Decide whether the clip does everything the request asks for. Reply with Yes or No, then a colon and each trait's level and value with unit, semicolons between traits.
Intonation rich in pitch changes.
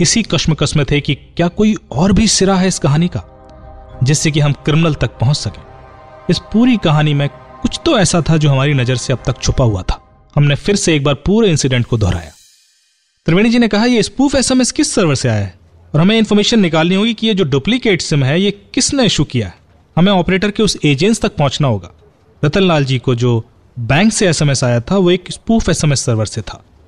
Yes: wide, 7.3 semitones